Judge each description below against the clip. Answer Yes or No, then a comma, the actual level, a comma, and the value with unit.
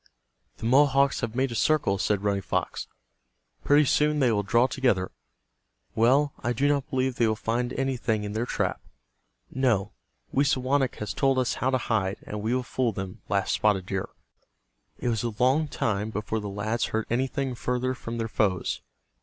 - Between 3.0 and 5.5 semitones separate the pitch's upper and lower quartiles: Yes, average, 3.9 semitones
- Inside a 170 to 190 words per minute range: Yes, average, 180 wpm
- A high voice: No, low, 120 Hz